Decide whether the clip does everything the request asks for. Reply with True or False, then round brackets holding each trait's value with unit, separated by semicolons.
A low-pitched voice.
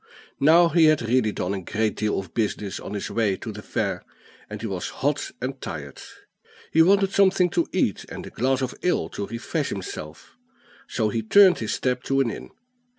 True (115 Hz)